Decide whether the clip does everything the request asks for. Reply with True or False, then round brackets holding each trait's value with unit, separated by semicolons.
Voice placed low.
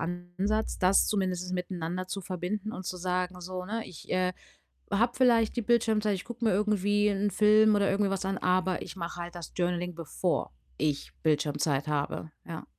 False (185 Hz)